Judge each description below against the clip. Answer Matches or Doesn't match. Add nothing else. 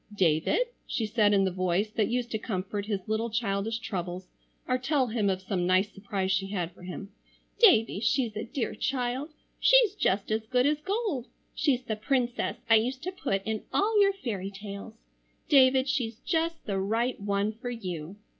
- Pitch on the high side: Matches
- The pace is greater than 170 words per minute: Matches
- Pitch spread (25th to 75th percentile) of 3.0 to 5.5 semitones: Matches